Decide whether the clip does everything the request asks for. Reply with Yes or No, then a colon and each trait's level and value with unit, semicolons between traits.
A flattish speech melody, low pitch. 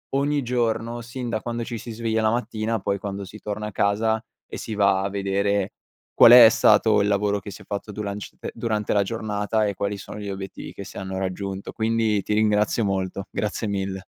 Yes: narrow, 2.0 semitones; low, 105 Hz